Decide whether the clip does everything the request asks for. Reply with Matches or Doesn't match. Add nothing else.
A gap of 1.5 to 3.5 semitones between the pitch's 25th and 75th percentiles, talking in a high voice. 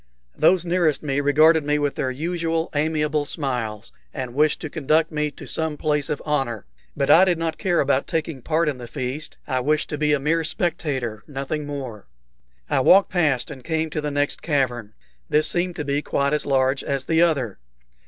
Doesn't match